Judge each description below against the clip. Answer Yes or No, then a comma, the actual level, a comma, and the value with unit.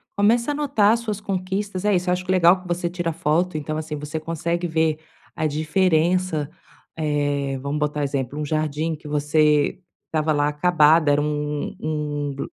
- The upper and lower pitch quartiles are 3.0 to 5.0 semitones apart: Yes, average, 3.4 semitones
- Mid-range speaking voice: Yes, medium, 155 Hz